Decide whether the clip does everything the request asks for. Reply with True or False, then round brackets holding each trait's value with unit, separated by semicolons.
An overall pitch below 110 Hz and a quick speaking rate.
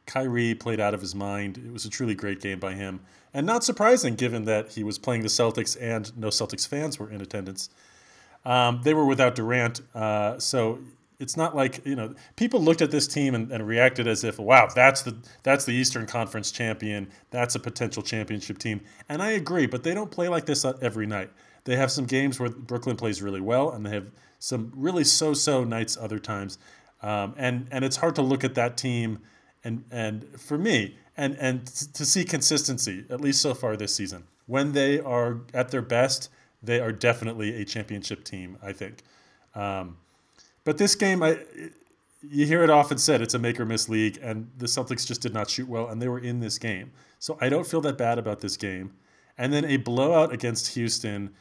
False (120 Hz; 210 wpm)